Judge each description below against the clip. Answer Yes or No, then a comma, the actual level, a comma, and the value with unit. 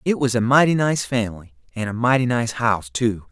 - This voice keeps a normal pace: No, fast, 215 wpm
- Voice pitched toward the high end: No, low, 120 Hz